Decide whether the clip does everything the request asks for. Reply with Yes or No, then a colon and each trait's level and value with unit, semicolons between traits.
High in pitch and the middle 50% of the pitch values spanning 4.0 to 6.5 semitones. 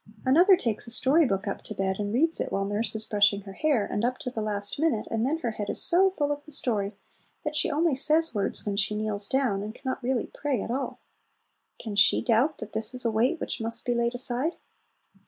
Yes: high, 235 Hz; wide, 5.4 semitones